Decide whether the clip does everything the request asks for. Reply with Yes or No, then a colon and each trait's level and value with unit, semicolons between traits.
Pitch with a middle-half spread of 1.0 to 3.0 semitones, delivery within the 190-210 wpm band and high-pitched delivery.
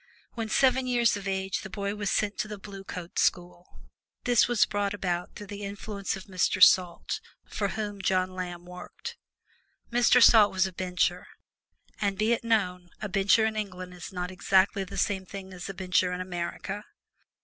No: narrow, 2.4 semitones; average, 180 wpm; high, 195 Hz